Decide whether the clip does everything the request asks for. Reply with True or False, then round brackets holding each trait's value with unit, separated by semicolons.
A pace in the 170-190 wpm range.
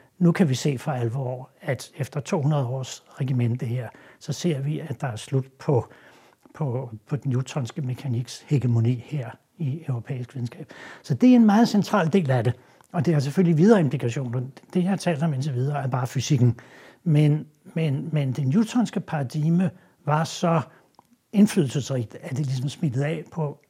True (180 wpm)